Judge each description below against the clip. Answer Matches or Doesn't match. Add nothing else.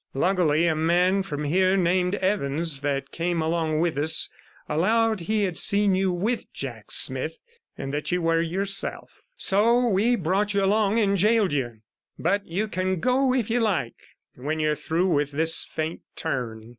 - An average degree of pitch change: Matches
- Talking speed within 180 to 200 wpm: Doesn't match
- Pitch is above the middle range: Doesn't match